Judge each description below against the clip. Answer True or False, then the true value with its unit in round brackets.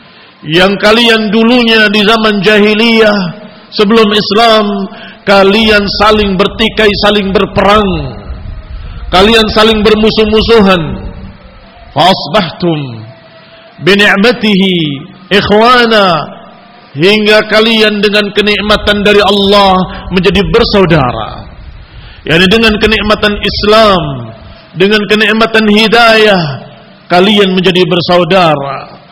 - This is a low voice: False (205 Hz)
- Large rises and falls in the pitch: False (2.7 semitones)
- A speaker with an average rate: False (80 wpm)